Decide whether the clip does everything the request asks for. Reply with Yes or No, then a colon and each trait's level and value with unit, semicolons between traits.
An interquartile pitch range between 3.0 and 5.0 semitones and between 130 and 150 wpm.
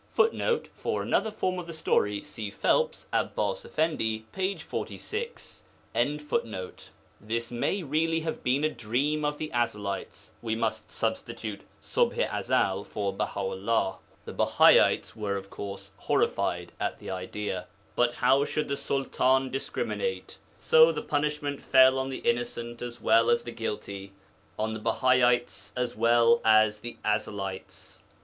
No: wide, 5.6 semitones; average, 140 wpm